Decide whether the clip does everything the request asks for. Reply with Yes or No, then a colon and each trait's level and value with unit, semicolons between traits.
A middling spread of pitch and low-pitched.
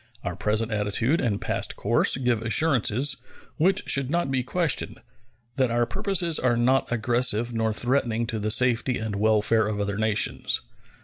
Yes: average, 3.2 semitones; low, 120 Hz